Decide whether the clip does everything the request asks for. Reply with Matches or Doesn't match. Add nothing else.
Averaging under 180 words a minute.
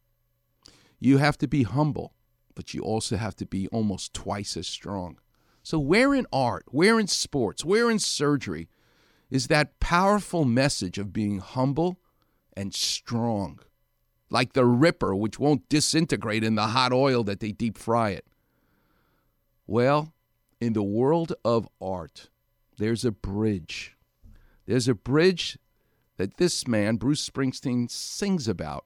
Matches